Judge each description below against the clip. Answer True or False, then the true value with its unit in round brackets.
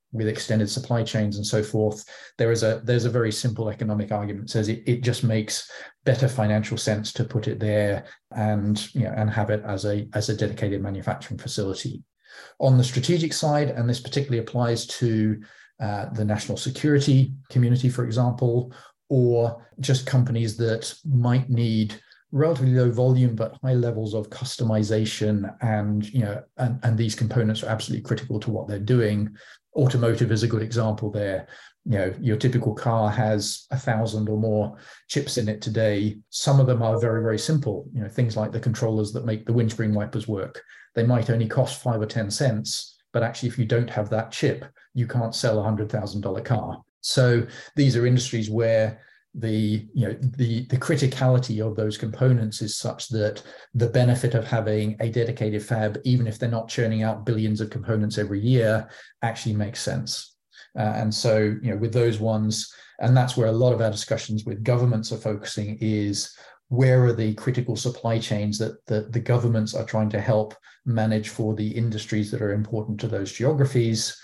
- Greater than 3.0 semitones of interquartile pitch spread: False (2.4 semitones)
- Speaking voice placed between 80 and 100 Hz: False (115 Hz)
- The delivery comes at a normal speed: True (185 wpm)